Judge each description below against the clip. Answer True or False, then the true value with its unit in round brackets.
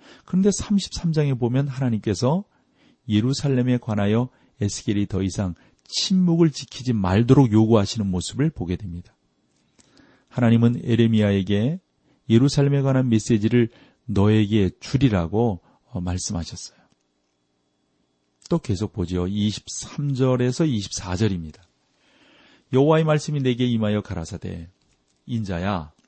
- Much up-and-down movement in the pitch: True (6.2 semitones)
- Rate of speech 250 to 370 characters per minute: True (260 characters per minute)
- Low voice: True (110 Hz)